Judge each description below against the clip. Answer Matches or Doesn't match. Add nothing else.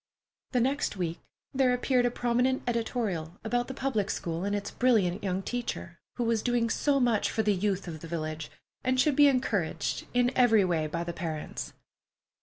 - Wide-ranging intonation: Matches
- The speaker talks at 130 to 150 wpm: Doesn't match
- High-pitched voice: Matches